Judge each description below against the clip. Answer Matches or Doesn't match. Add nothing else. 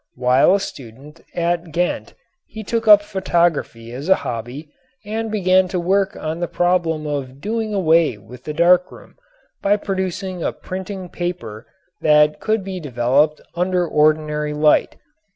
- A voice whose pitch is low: Doesn't match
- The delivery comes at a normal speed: Matches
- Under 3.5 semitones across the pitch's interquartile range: Doesn't match